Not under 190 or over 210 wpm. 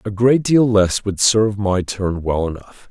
Yes: fast, 205 wpm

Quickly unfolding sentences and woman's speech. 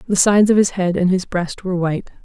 Yes: fast, 270 wpm; female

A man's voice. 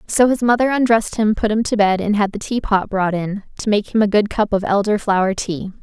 No: female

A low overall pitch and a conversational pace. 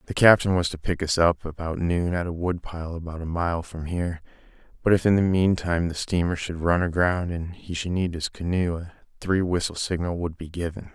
No: very low, 85 Hz; fast, 225 wpm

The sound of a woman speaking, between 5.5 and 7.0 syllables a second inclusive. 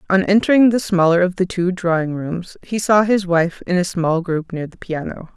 No: female; 5.0 syllables/s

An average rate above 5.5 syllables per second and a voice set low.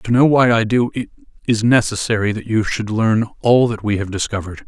Yes: 5.7 syllables/s; low, 110 Hz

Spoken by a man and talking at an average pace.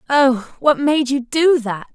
No: female; average, 185 wpm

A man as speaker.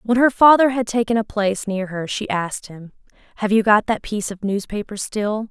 No: female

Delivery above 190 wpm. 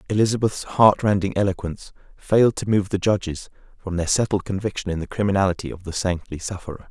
No: average, 175 wpm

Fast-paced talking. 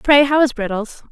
Yes: fast, 215 wpm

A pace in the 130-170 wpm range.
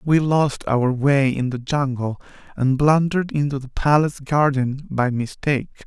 Yes: average, 155 wpm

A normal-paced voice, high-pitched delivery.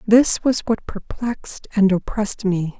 Yes: average, 150 wpm; high, 210 Hz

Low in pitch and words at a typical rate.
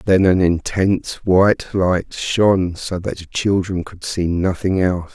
Yes: very low, 90 Hz; average, 165 wpm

